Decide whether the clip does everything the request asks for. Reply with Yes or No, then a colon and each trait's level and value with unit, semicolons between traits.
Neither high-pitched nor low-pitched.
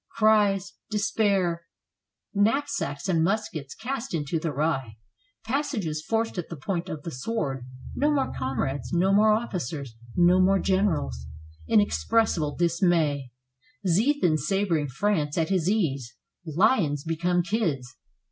Yes: medium, 175 Hz